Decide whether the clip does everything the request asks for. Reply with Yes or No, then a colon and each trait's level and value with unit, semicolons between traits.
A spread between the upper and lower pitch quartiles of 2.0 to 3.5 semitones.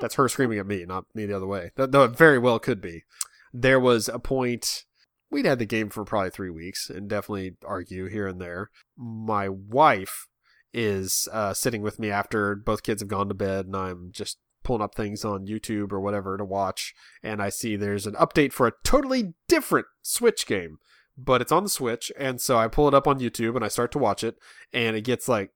No: average, 3.9 semitones